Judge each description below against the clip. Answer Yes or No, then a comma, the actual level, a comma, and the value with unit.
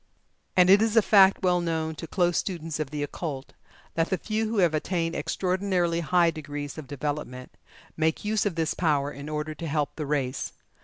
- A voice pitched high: No, medium, 165 Hz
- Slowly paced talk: No, average, 195 wpm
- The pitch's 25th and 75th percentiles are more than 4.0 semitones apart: No, average, 3.4 semitones